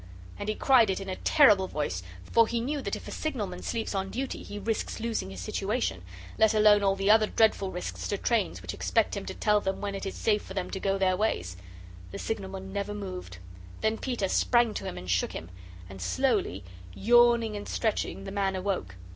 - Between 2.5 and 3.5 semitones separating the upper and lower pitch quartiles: Yes, average, 3.2 semitones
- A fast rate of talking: Yes, fast, 215 wpm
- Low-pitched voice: No, high, 200 Hz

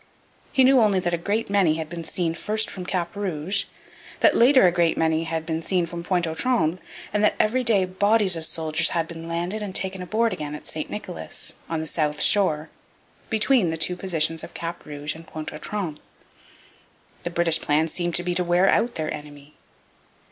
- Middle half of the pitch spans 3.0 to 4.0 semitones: Yes, average, 3.7 semitones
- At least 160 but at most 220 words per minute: Yes, fast, 205 wpm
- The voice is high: No, medium, 175 Hz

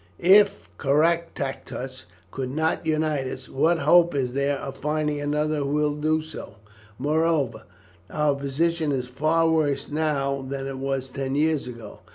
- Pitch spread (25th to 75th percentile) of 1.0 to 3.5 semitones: Yes, narrow, 2.6 semitones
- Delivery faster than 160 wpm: No, average, 150 wpm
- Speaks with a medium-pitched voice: Yes, medium, 145 Hz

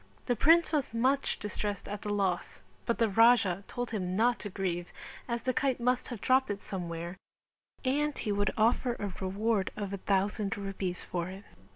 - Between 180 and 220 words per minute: Yes, average, 185 wpm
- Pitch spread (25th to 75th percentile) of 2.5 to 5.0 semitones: Yes, average, 4.0 semitones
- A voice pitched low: No, high, 205 Hz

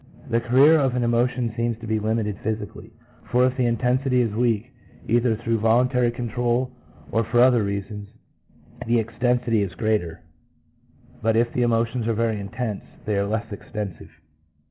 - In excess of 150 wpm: Yes, average, 165 wpm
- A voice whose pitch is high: No, low, 115 Hz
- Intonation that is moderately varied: No, narrow, 2.1 semitones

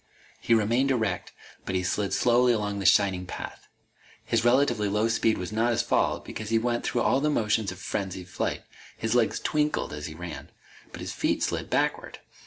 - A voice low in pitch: Yes, low, 110 Hz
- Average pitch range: Yes, average, 3.7 semitones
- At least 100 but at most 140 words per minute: No, average, 195 wpm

